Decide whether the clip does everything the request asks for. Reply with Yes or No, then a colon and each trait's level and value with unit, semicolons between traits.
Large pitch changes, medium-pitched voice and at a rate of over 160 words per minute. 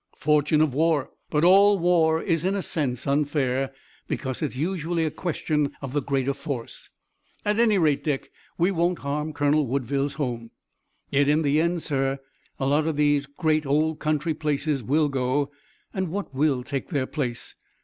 No: average, 2.7 semitones; medium, 150 Hz; average, 170 wpm